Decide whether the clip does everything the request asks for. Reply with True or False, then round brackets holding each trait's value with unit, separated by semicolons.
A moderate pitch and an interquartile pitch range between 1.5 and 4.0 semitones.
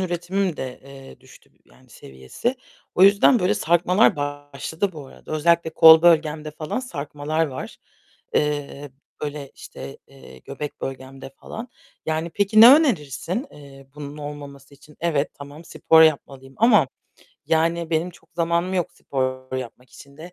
True (150 Hz; 3.6 semitones)